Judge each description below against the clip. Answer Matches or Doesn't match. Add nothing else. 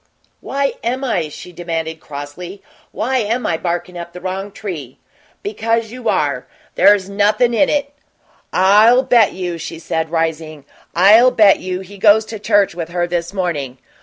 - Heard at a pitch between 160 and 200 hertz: Matches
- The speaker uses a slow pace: Doesn't match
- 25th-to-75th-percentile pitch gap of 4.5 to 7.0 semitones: Matches